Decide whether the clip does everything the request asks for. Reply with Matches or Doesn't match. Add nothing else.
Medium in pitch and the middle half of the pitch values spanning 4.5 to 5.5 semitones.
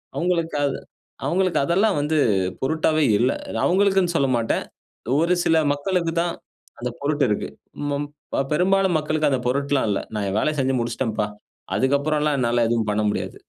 Matches